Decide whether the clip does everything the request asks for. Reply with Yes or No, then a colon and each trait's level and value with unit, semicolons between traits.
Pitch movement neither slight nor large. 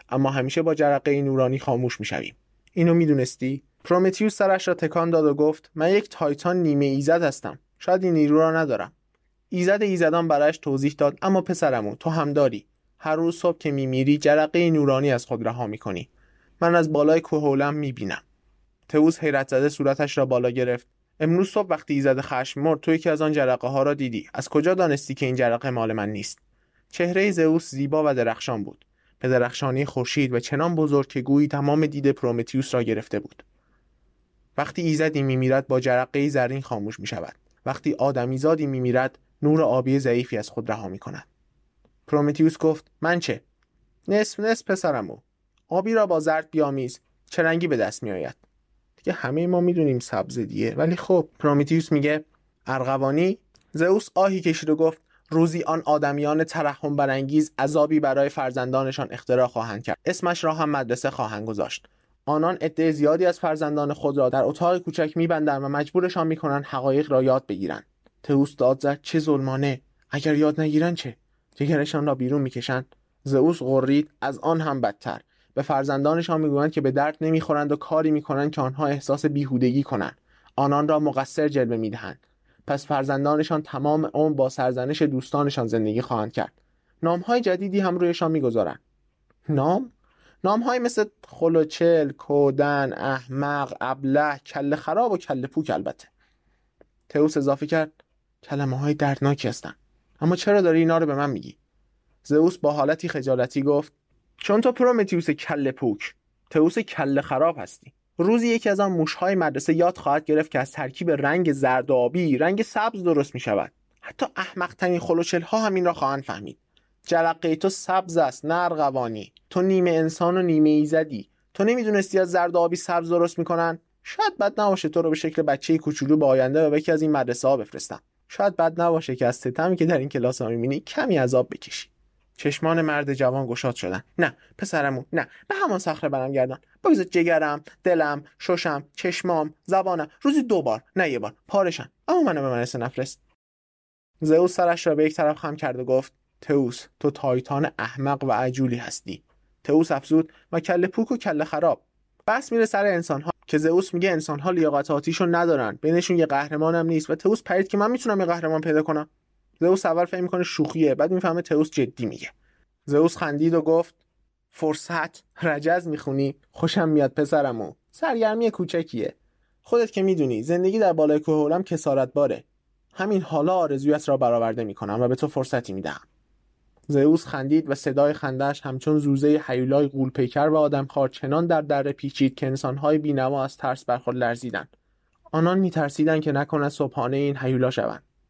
Yes: average, 3.7 semitones